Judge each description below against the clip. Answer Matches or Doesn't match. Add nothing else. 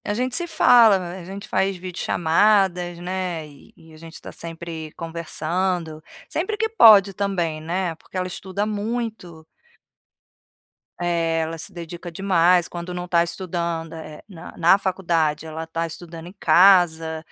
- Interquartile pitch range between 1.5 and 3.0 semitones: Matches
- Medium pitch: Matches